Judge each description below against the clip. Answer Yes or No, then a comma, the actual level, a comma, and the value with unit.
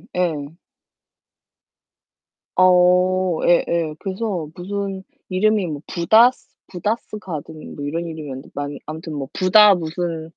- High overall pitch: No, medium, 175 Hz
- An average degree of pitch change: Yes, average, 3.1 semitones